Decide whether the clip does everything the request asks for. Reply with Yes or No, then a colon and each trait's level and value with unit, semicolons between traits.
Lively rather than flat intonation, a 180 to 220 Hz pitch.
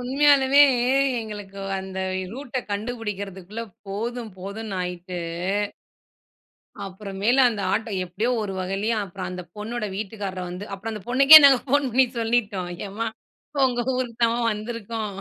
No: average, 3.8 semitones; high, 215 Hz